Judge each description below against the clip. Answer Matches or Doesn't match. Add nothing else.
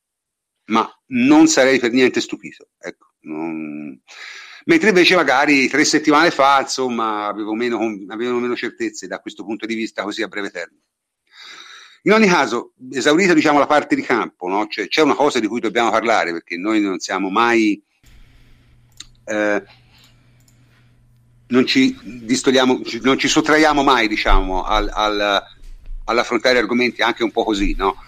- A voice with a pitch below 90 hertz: Doesn't match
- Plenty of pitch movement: Matches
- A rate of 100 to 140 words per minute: Doesn't match